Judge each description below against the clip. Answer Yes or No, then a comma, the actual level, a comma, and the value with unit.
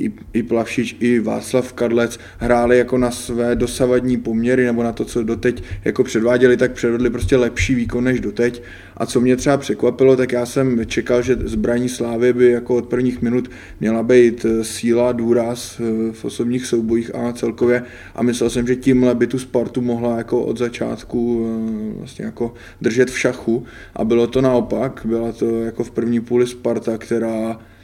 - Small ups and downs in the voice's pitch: Yes, narrow, 1.2 semitones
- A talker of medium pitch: No, low, 120 Hz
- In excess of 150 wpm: Yes, fast, 170 wpm